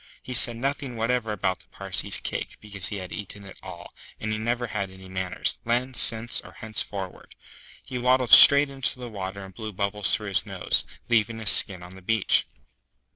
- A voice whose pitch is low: Yes, low, 110 Hz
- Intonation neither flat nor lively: Yes, average, 3.8 semitones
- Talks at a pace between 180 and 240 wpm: Yes, average, 190 wpm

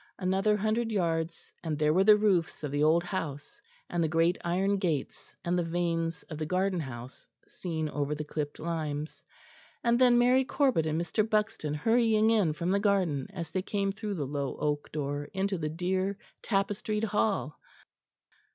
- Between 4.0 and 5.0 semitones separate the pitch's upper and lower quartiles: Yes, average, 4.7 semitones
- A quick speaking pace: No, average, 175 wpm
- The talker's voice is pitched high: No, medium, 175 Hz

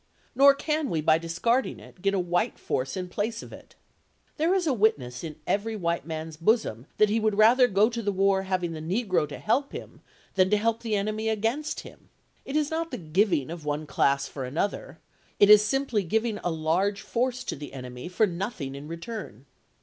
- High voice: Yes, high, 200 Hz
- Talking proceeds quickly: Yes, fast, 210 wpm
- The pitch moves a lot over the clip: Yes, wide, 5.8 semitones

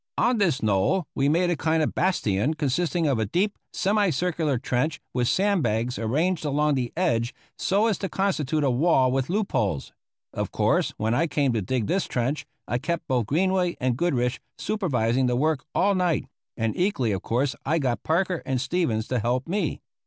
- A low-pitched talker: No, medium, 145 Hz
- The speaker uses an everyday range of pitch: No, wide, 6.3 semitones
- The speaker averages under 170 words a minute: No, average, 190 wpm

